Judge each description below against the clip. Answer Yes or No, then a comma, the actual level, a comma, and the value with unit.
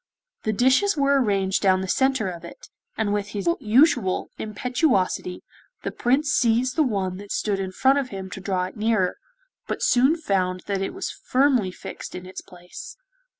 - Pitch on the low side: No, high, 210 Hz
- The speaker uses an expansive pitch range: Yes, wide, 5.7 semitones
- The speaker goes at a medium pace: Yes, average, 180 wpm